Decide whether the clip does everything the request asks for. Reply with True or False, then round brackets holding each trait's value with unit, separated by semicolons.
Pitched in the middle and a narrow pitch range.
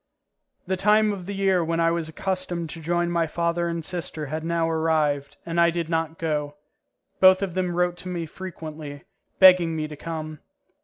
True (170 Hz; 2.0 semitones)